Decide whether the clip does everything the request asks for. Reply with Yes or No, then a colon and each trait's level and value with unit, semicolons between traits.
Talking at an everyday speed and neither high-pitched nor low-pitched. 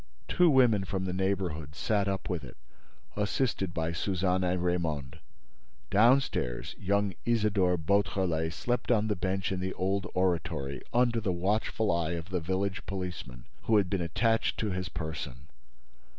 No: average, 150 wpm; very low, 95 Hz